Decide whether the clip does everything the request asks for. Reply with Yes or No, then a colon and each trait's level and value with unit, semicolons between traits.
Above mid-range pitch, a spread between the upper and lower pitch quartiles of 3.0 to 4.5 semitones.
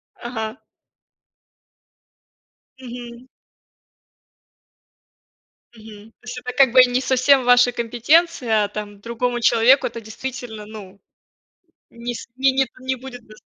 No: high, 245 Hz; narrow, 2.6 semitones